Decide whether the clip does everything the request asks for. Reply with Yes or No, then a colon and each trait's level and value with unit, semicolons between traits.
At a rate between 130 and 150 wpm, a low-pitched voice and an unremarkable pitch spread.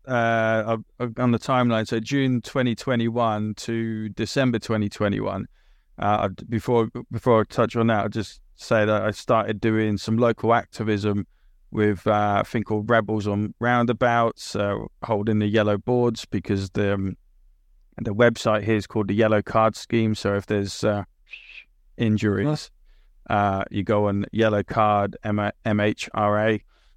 No: average, 145 wpm; low, 110 Hz; narrow, 1.9 semitones